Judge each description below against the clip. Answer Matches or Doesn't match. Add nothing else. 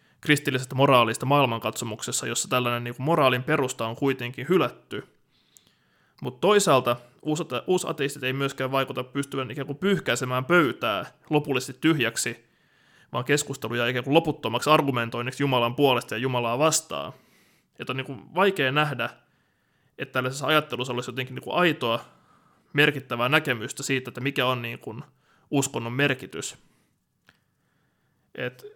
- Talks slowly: Doesn't match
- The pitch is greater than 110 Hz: Matches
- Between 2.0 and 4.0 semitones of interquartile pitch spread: Matches